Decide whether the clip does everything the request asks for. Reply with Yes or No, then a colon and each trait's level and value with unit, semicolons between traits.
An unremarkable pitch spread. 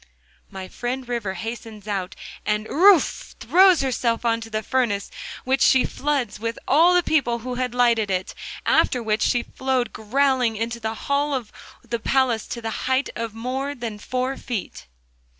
Yes: average, 3.0 semitones